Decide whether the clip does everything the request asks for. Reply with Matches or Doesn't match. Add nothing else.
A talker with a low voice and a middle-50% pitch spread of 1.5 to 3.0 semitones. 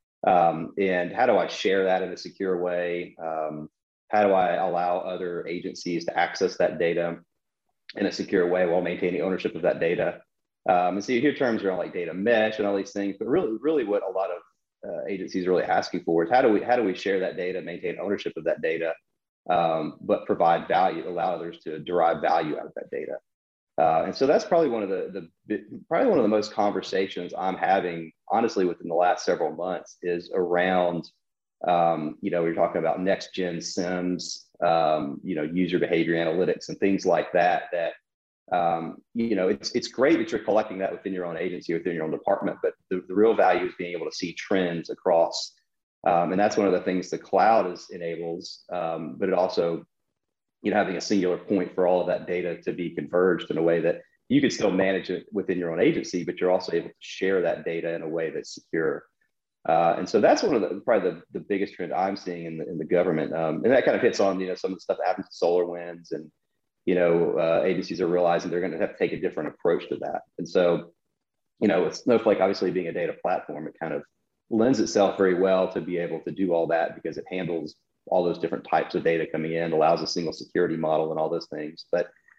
Matches